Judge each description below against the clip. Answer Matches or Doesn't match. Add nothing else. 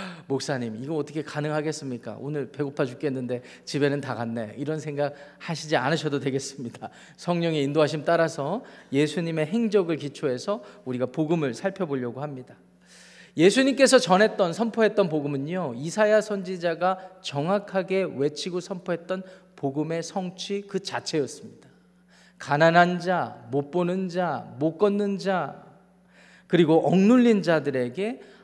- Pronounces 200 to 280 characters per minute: Doesn't match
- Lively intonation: Doesn't match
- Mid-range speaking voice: Matches